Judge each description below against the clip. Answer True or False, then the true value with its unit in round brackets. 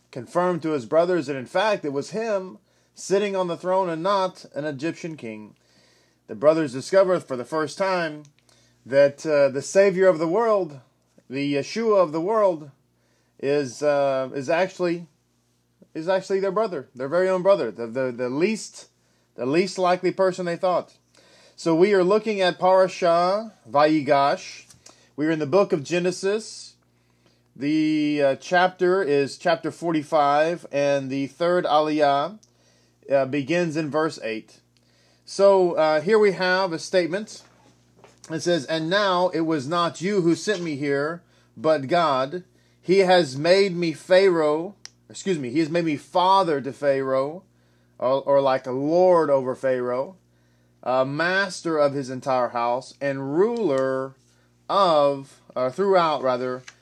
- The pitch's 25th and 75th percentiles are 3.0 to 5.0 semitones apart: False (5.5 semitones)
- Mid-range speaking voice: True (155 Hz)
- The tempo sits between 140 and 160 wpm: True (150 wpm)